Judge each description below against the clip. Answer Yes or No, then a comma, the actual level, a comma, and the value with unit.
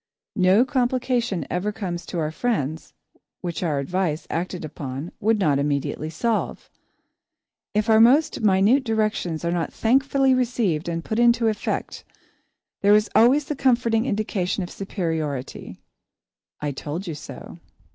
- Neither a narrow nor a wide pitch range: No, wide, 6.2 semitones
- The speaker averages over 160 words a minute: No, slow, 135 wpm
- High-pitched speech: Yes, high, 195 Hz